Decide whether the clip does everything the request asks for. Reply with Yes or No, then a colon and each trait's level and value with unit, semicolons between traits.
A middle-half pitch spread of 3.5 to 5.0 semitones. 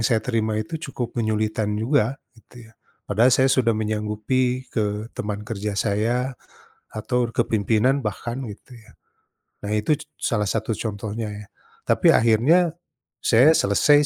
No: average, 2.9 semitones